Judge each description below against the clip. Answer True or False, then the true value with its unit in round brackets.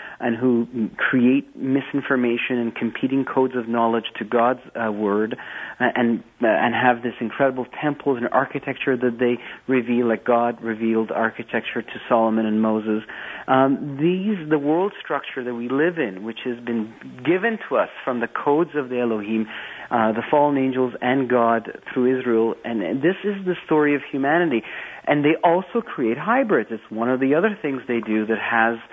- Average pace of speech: True (180 wpm)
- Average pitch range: True (3.4 semitones)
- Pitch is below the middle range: True (125 Hz)